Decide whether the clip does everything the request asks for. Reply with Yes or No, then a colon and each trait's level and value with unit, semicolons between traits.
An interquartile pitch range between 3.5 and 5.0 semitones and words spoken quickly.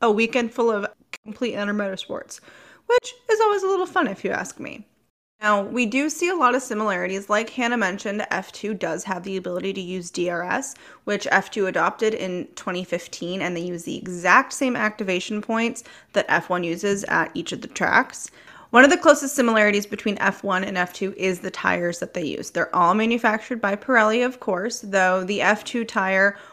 No: average, 4.1 semitones; average, 190 wpm